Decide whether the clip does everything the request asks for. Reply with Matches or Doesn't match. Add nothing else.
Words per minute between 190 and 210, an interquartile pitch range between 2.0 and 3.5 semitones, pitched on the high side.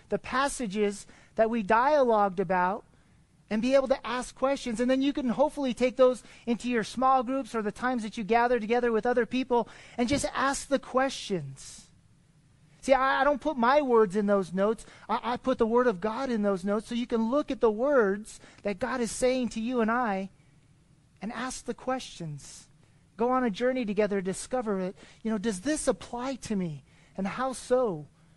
Doesn't match